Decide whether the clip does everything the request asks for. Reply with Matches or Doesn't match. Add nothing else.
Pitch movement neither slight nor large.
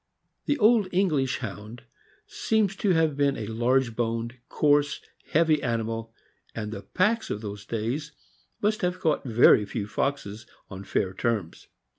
Doesn't match